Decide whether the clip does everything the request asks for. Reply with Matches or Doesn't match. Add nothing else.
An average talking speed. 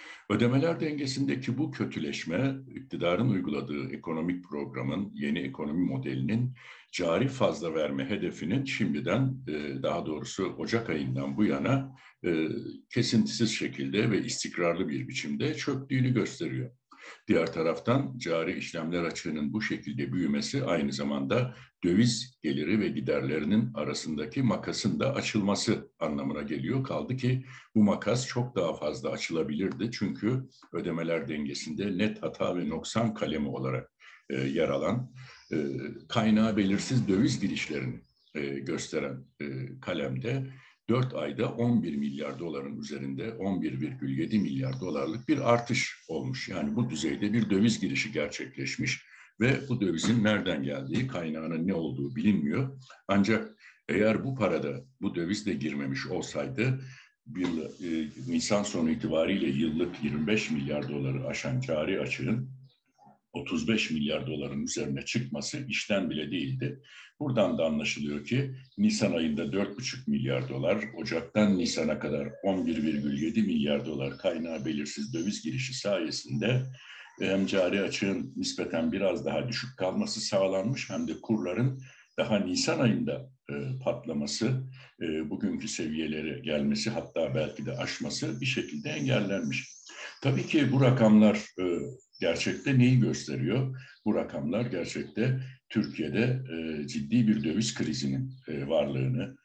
Matches